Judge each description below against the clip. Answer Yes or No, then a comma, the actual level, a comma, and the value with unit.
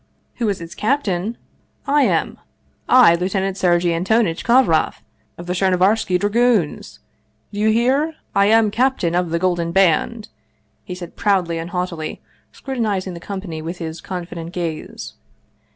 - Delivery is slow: No, average, 150 wpm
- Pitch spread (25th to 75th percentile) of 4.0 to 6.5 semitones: Yes, average, 4.3 semitones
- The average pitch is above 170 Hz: Yes, medium, 185 Hz